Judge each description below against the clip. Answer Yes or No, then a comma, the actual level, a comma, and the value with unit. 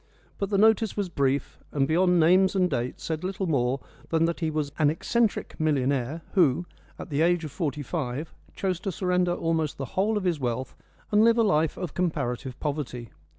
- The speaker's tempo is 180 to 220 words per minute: Yes, average, 195 wpm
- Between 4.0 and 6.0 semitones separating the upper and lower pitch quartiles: Yes, average, 4.7 semitones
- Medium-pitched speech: Yes, medium, 160 Hz